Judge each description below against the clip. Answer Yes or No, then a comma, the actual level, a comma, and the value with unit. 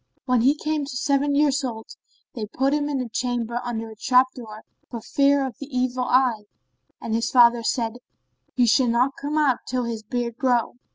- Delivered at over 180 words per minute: Yes, average, 195 wpm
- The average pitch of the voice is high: Yes, very high, 250 Hz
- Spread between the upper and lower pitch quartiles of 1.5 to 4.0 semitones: Yes, average, 2.8 semitones